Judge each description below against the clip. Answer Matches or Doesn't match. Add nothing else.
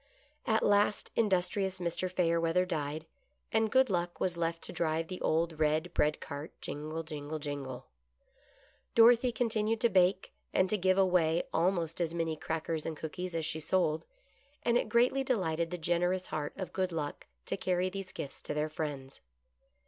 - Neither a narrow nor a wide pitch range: Matches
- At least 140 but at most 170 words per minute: Matches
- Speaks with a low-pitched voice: Doesn't match